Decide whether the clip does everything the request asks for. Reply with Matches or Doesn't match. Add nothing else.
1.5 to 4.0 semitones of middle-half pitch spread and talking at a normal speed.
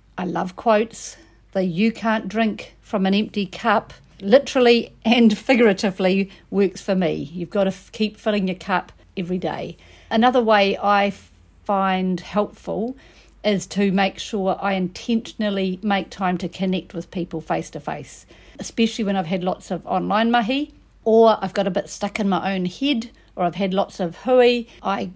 Matches